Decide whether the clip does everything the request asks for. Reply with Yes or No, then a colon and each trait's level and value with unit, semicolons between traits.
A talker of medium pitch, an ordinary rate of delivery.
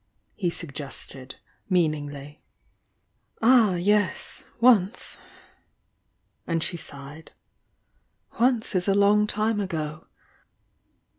No: medium, 180 Hz; slow, 80 wpm